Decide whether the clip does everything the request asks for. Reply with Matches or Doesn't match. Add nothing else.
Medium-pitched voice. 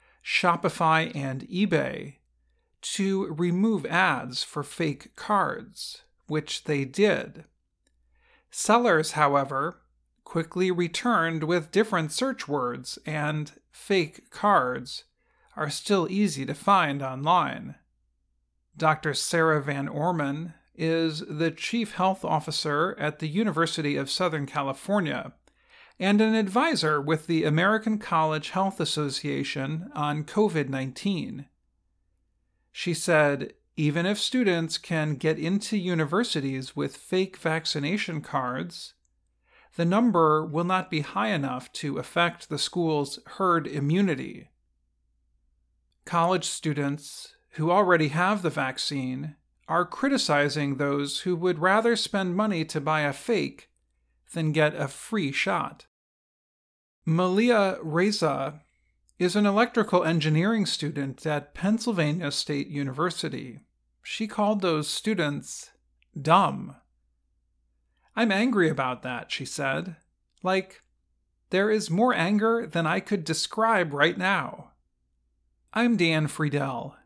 Matches